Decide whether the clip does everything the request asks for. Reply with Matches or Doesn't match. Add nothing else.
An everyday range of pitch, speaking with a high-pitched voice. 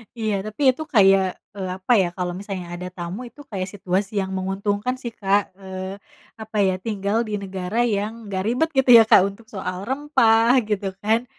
Matches